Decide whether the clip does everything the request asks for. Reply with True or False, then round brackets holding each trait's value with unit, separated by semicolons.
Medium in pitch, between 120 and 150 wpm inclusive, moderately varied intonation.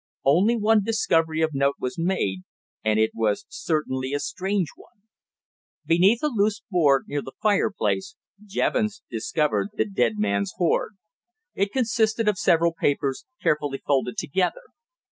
False (170 Hz; 140 wpm; 7.0 semitones)